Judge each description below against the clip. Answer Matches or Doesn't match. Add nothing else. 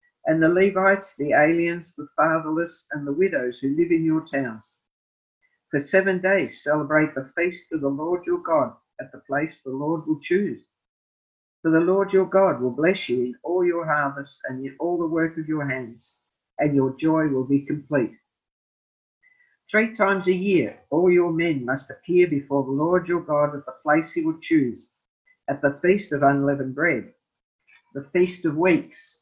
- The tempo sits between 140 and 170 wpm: Doesn't match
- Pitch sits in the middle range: Matches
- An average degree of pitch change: Matches